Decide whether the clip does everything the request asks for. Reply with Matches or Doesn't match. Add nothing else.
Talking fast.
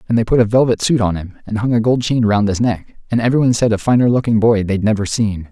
Matches